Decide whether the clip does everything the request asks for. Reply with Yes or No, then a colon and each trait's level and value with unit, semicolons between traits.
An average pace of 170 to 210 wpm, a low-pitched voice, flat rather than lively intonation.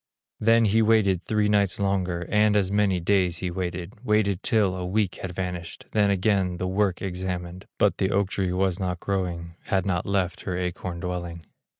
Yes: average, 185 wpm; very low, 95 Hz; narrow, 2.2 semitones